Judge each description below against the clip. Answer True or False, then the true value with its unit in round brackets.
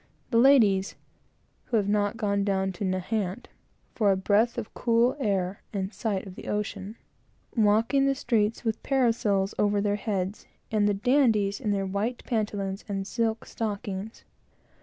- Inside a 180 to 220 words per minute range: False (155 wpm)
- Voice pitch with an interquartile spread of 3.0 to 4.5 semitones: False (2.5 semitones)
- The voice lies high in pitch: True (210 Hz)